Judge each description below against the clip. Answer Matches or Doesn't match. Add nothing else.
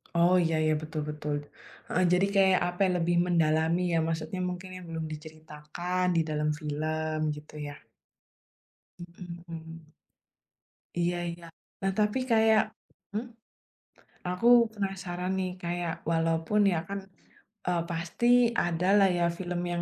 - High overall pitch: Doesn't match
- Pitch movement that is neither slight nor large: Doesn't match